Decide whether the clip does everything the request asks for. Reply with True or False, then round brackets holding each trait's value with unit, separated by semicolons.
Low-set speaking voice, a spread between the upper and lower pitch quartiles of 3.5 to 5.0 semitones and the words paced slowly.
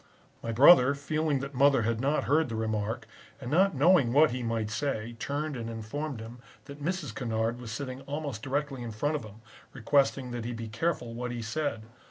False (125 Hz; 4.1 semitones; 200 wpm)